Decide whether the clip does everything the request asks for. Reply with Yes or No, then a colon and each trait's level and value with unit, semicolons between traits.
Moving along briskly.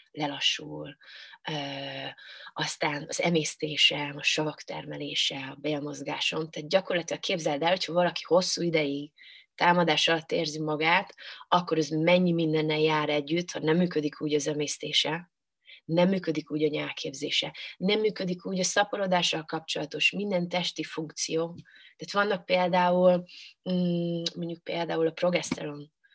No: average, 125 wpm